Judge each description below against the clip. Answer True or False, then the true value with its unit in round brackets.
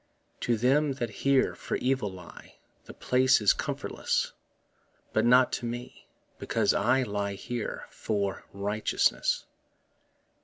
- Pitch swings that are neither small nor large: True (4.0 semitones)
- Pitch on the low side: True (120 Hz)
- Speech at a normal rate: False (125 wpm)